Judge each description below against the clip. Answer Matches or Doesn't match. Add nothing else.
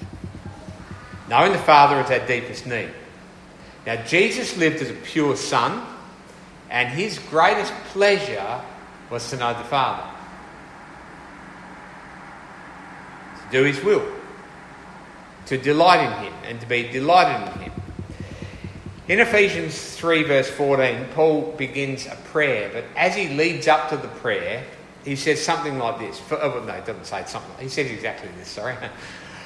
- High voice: Doesn't match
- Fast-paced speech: Doesn't match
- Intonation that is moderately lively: Doesn't match